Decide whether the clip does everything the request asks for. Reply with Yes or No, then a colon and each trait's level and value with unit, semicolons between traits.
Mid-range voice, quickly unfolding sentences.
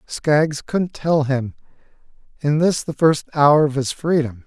No: medium, 150 Hz; average, 175 wpm